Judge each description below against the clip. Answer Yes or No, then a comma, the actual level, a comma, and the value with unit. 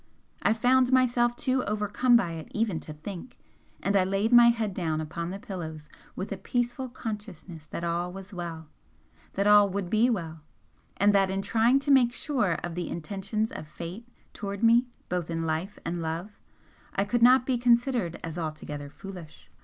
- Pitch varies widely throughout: Yes, wide, 5.7 semitones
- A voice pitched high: Yes, high, 200 Hz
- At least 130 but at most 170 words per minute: No, average, 180 wpm